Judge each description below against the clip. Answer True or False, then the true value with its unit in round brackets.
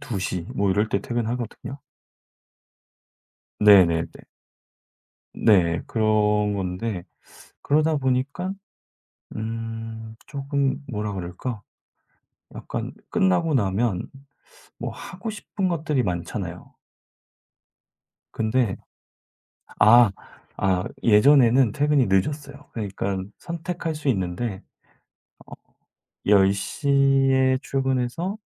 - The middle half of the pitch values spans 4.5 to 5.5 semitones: False (5.9 semitones)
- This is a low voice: True (115 Hz)